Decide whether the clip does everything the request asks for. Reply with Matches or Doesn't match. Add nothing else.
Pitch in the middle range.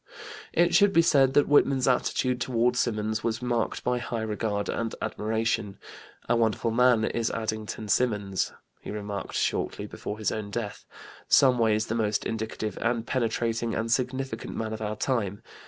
Doesn't match